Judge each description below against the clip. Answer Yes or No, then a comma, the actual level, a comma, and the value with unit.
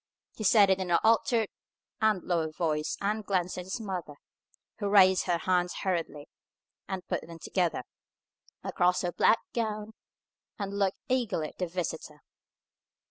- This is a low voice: No, medium, 185 Hz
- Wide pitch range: No, average, 3.2 semitones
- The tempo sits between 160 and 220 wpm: No, average, 150 wpm